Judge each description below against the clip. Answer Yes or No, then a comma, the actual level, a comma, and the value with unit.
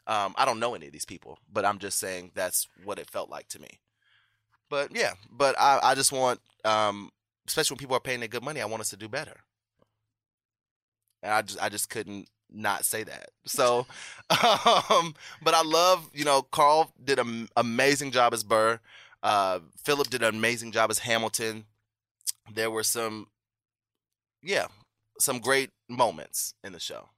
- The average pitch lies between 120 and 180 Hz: No, low, 110 Hz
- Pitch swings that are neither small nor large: Yes, average, 3.0 semitones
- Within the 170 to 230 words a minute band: Yes, average, 180 wpm